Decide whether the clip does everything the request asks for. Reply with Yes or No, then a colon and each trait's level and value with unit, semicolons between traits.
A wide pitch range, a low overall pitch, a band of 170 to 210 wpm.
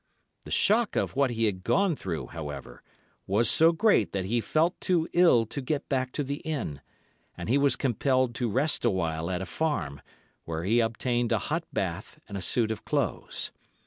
Yes: wide, 7.1 semitones; low, 120 Hz; average, 190 wpm